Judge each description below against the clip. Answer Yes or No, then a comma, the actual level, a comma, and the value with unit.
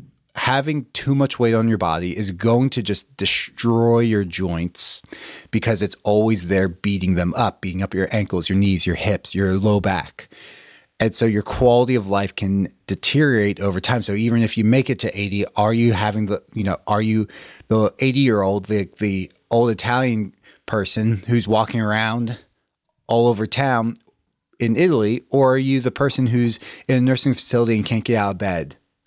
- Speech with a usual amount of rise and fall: Yes, average, 3.1 semitones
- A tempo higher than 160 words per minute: Yes, average, 190 wpm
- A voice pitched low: Yes, low, 110 Hz